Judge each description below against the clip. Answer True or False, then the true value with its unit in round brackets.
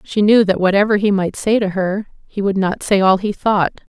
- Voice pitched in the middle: False (200 Hz)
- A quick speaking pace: True (245 wpm)